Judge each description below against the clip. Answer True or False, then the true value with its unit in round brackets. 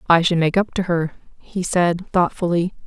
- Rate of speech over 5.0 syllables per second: False (4.8 syllables/s)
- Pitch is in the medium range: True (175 Hz)